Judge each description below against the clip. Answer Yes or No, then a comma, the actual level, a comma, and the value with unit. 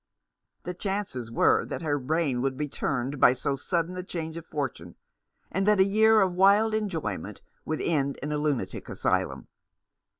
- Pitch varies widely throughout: Yes, wide, 5.9 semitones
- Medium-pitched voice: Yes, medium, 160 Hz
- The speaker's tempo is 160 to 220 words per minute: Yes, average, 175 wpm